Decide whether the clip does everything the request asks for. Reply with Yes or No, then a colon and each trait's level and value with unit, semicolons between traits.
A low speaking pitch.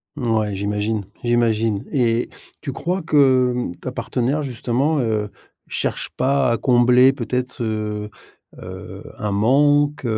Yes: low, 120 Hz